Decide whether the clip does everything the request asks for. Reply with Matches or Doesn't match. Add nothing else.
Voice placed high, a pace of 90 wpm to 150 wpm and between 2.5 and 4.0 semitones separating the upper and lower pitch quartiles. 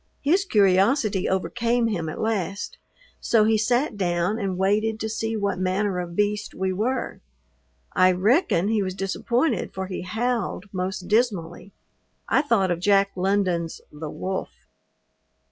Matches